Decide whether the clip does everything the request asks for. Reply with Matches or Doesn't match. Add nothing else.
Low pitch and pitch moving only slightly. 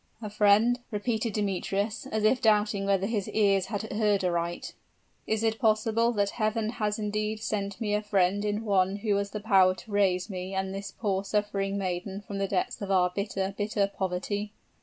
Doesn't match